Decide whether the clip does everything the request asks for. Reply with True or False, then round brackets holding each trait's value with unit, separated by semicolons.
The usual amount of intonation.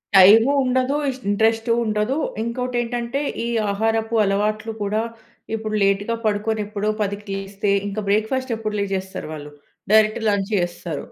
False (2.1 semitones)